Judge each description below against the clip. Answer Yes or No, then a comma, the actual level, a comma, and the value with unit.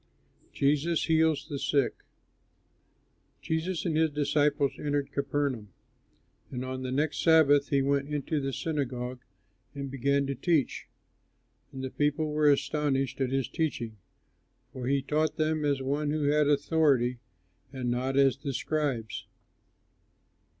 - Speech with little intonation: Yes, narrow, 2.1 semitones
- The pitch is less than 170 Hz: Yes, medium, 140 Hz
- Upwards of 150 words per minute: No, slow, 135 wpm